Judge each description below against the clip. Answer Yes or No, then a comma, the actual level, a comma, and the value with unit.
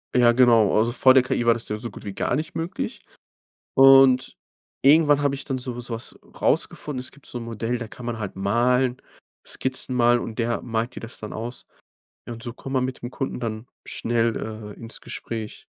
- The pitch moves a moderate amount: No, narrow, 2.3 semitones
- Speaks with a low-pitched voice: Yes, low, 120 Hz